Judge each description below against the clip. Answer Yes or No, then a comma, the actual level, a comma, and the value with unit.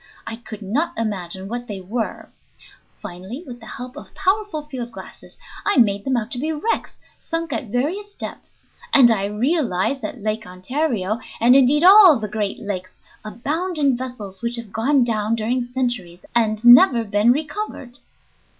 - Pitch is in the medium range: No, high, 240 Hz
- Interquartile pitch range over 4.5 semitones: Yes, average, 5.1 semitones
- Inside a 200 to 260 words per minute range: No, average, 165 wpm